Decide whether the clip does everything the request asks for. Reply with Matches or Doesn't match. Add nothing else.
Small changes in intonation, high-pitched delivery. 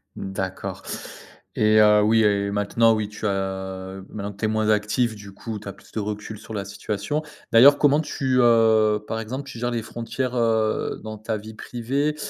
Doesn't match